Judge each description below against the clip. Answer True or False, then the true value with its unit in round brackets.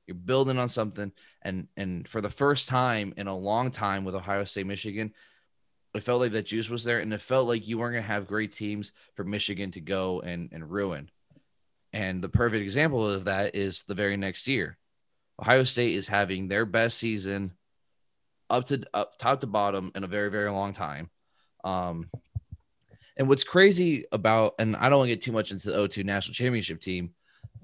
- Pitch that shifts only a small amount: False (3.2 semitones)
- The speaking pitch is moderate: False (105 Hz)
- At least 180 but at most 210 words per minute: True (200 wpm)